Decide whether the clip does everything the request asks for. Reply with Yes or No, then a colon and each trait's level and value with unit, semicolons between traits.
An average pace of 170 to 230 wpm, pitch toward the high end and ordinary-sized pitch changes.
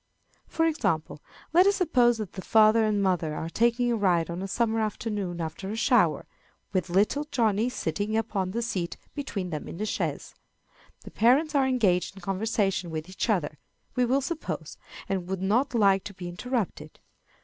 Yes: average, 180 wpm; high, 205 Hz; average, 4.7 semitones